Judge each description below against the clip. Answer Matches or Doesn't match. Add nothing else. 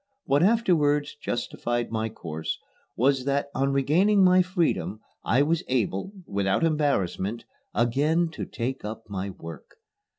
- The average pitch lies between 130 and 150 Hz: Matches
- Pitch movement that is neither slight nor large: Doesn't match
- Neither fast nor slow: Doesn't match